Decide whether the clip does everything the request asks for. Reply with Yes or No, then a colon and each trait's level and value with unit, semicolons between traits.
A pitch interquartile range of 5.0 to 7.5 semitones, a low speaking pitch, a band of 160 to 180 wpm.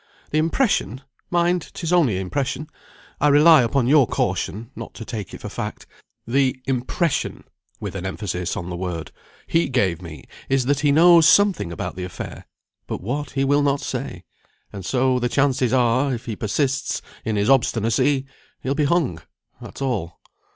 Yes: wide, 5.6 semitones; low, 130 Hz; average, 170 wpm